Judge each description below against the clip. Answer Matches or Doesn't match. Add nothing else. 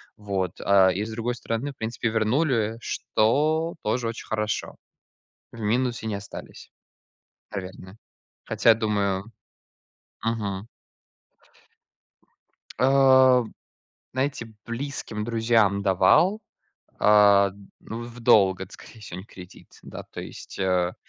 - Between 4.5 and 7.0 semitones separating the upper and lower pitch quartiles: Doesn't match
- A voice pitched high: Doesn't match